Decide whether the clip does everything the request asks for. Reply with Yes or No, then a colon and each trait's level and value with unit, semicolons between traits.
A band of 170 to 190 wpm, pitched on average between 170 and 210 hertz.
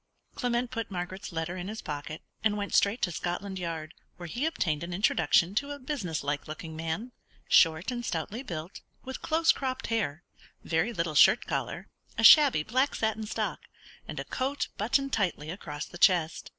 Yes: average, 175 wpm; high, 190 Hz